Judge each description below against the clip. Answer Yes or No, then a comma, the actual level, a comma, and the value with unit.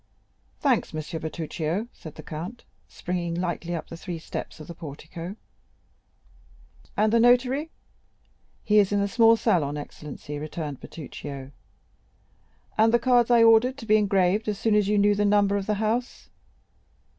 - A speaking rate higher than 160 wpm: No, average, 155 wpm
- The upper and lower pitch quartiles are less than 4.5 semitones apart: No, average, 5.3 semitones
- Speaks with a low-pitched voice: No, high, 200 Hz